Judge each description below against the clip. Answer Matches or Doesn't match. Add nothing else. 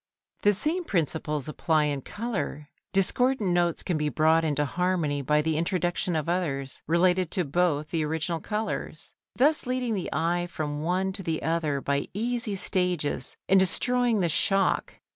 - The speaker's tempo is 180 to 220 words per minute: Doesn't match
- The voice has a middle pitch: Matches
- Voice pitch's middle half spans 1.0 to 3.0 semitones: Doesn't match